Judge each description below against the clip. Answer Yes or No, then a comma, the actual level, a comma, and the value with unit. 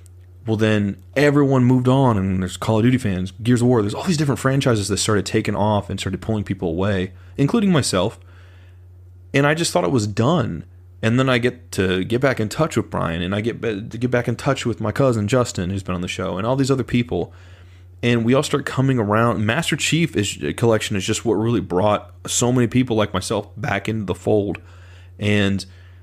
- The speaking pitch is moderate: No, low, 105 Hz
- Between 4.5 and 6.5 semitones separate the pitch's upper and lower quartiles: Yes, average, 5.2 semitones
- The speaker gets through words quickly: Yes, fast, 220 wpm